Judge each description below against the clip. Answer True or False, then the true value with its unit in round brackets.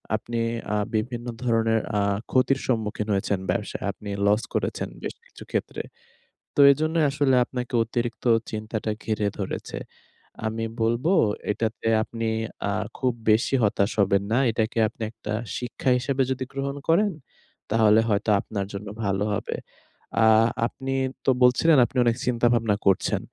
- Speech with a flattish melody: False (3.1 semitones)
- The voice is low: True (115 Hz)